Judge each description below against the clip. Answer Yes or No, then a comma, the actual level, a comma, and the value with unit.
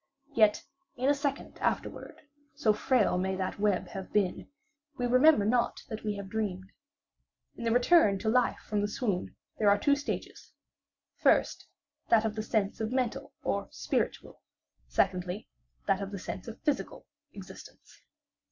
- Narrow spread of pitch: No, average, 3.7 semitones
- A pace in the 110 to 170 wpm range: Yes, average, 155 wpm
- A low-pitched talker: No, high, 215 Hz